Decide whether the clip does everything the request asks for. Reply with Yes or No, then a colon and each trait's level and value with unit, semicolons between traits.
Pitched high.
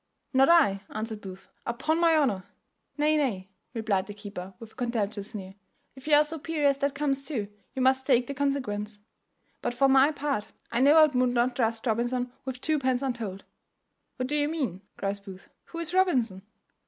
Yes: very high, 255 Hz